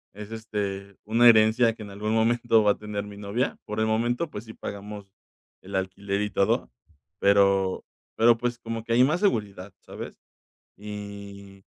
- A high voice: No, low, 105 Hz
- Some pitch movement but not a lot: No, narrow, 2.3 semitones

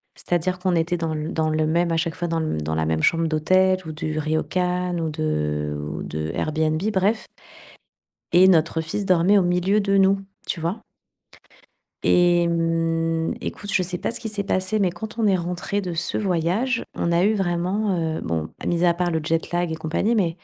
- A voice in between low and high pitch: Yes, medium, 170 Hz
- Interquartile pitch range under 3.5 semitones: Yes, average, 2.8 semitones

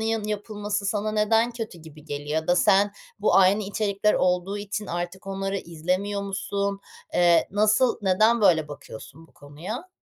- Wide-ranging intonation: No, average, 3.2 semitones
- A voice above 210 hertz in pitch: No, high, 200 Hz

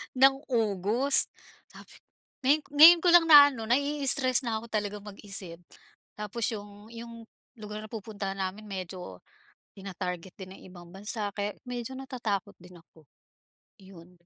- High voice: Yes, high, 210 Hz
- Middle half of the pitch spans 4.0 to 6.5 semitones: Yes, average, 4.3 semitones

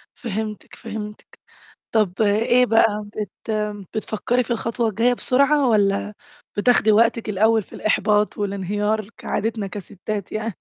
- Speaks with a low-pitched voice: No, high, 215 Hz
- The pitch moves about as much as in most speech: No, narrow, 1.8 semitones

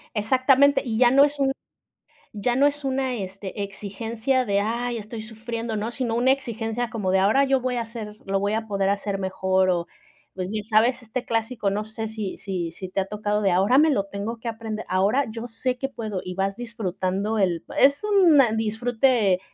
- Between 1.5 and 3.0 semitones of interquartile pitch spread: No, average, 3.6 semitones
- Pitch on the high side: Yes, high, 220 Hz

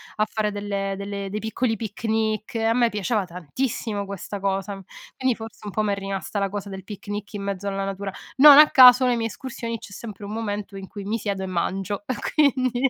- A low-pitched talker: No, high, 205 Hz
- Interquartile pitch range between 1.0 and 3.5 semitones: Yes, narrow, 2.4 semitones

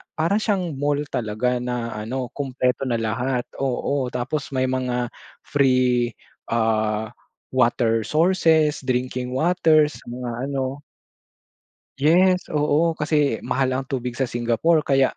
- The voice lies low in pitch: Yes, low, 130 Hz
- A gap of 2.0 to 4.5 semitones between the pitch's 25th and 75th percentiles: Yes, average, 3.4 semitones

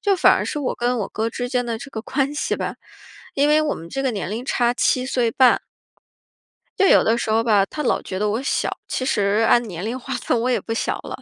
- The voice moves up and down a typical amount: Yes, average, 3.3 semitones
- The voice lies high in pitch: Yes, high, 240 Hz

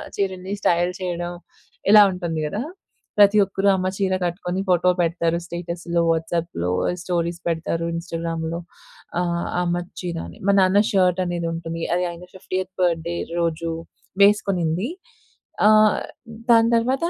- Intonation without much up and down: Yes, narrow, 2.0 semitones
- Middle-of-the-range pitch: Yes, medium, 175 Hz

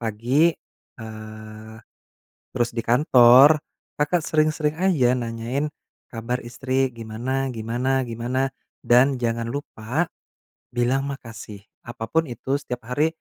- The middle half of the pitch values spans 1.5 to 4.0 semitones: Yes, average, 3.2 semitones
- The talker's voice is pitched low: Yes, low, 125 Hz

